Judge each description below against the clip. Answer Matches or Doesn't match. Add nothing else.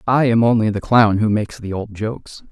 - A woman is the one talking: Doesn't match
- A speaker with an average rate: Doesn't match